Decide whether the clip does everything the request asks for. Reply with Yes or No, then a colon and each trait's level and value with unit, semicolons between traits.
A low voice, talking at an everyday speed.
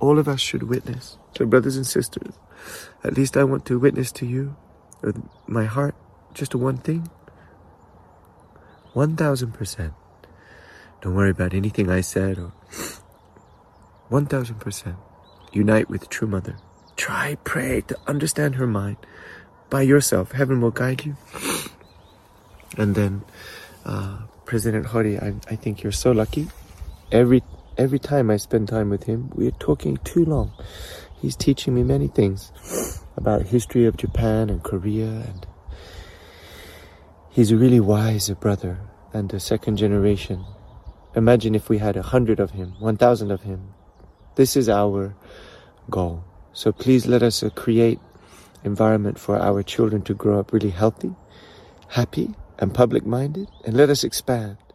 Yes: low, 105 Hz; average, 145 wpm